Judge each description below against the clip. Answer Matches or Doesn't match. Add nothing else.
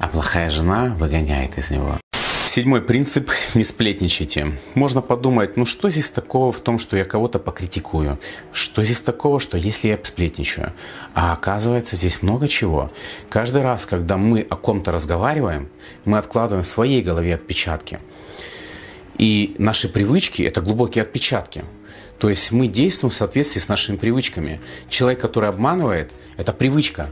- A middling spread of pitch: Doesn't match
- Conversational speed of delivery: Matches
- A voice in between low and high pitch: Doesn't match